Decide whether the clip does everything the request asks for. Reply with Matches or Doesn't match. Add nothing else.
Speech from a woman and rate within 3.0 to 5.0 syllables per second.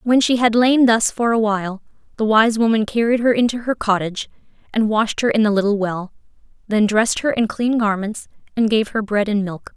Doesn't match